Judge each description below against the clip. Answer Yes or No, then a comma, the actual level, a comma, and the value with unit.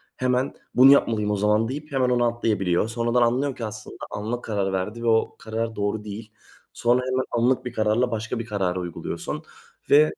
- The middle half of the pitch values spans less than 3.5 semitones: Yes, average, 2.9 semitones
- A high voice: No, low, 115 Hz